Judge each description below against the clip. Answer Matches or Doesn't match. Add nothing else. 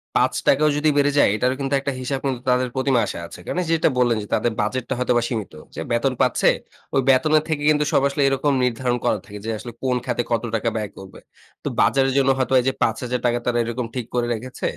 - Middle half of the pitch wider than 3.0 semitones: Doesn't match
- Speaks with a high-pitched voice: Doesn't match